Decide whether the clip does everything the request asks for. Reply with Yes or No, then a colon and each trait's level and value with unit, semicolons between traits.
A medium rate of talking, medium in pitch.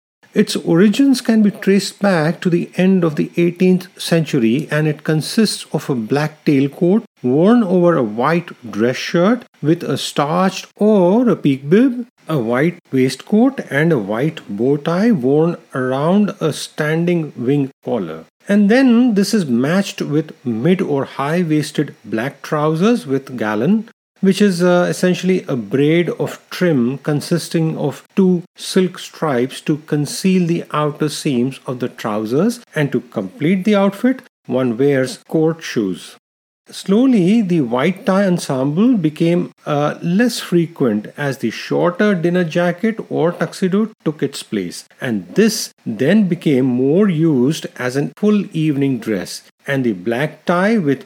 Yes: average, 145 wpm; medium, 170 Hz